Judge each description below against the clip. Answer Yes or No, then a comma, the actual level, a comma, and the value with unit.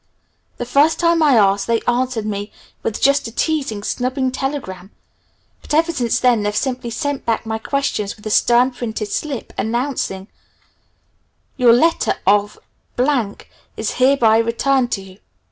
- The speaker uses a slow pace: No, average, 145 wpm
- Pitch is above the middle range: Yes, high, 240 Hz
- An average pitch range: Yes, average, 4.2 semitones